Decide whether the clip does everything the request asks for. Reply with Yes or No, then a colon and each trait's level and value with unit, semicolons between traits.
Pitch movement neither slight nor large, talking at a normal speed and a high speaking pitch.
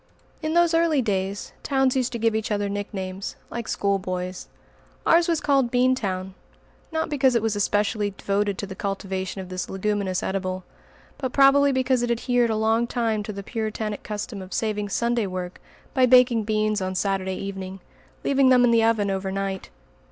Yes: average, 4.2 semitones; average, 180 wpm; high, 215 Hz